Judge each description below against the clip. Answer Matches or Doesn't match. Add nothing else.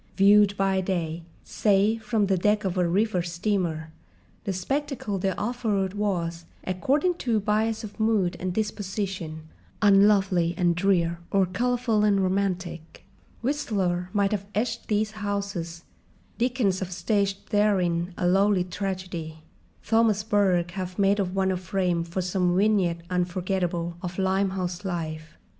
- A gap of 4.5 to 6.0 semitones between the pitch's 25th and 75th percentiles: Doesn't match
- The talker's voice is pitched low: Doesn't match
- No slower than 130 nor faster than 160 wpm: Matches